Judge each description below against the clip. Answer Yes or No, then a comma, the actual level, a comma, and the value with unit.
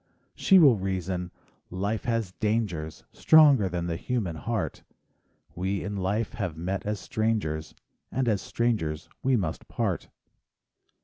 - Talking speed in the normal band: No, slow, 130 wpm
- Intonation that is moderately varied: Yes, average, 4.4 semitones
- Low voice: Yes, low, 100 Hz